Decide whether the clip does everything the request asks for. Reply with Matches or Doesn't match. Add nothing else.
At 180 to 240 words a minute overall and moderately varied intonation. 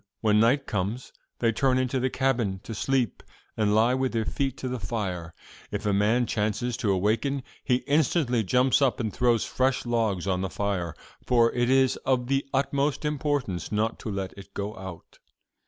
Matches